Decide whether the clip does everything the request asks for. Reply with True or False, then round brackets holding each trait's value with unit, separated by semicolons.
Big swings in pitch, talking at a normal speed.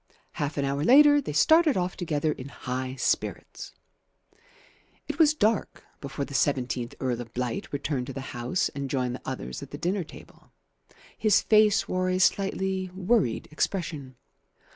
True (6.7 semitones; 160 wpm)